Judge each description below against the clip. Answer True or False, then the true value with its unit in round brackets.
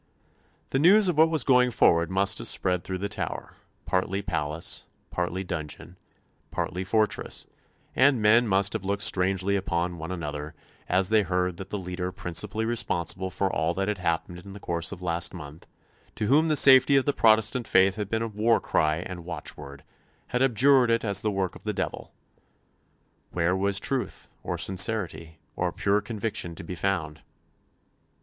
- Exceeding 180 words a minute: False (175 wpm)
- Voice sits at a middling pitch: False (95 Hz)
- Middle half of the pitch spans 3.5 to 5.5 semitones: True (4.1 semitones)